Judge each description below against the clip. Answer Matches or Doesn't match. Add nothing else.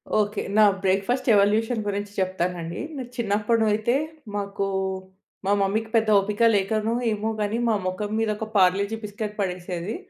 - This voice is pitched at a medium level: Doesn't match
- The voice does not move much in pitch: Matches